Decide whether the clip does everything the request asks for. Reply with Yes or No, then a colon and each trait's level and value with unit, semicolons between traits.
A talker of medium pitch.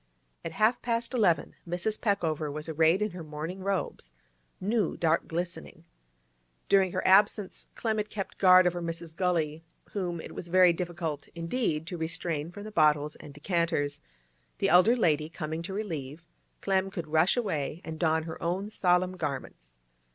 Yes: medium, 170 Hz